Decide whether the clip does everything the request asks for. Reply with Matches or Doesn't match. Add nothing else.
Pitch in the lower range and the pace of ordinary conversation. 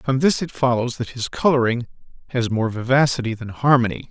Matches